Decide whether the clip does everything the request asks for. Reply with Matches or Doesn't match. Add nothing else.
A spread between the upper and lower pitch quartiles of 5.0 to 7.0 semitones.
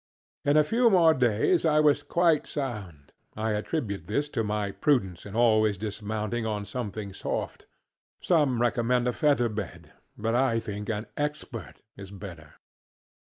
Matches